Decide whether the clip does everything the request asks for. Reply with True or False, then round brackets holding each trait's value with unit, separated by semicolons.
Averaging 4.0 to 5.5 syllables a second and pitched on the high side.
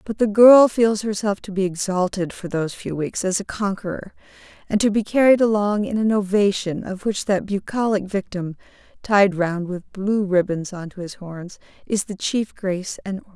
True (5.0 syllables/s; 195 Hz)